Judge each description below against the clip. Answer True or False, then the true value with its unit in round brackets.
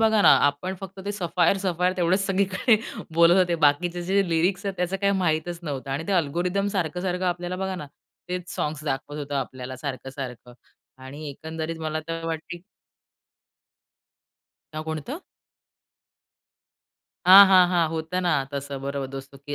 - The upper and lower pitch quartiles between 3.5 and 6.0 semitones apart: True (4.0 semitones)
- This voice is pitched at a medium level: True (170 Hz)